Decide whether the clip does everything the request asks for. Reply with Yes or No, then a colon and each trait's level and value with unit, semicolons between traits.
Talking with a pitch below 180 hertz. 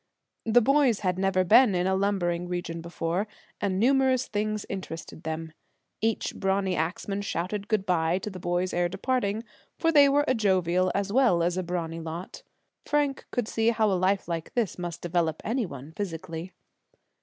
No: high, 190 Hz